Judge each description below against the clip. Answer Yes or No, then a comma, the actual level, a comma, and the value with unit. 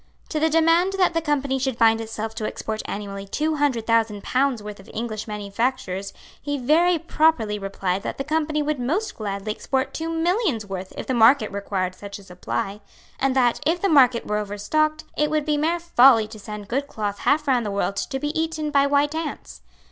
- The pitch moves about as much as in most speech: No, wide, 6.5 semitones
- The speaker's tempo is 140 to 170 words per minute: No, average, 200 wpm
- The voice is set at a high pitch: Yes, very high, 255 Hz